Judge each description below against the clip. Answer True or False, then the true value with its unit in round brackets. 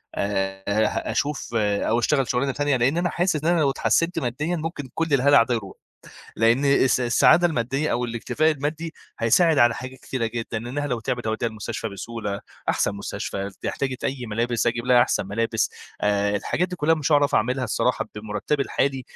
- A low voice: True (125 Hz)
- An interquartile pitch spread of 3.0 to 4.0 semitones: False (4.4 semitones)